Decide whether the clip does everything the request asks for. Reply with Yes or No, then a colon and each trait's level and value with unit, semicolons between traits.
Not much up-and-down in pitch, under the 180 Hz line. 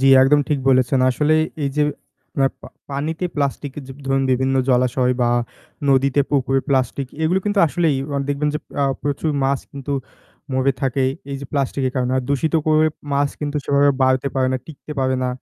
Yes: narrow, 2.0 semitones; medium, 140 Hz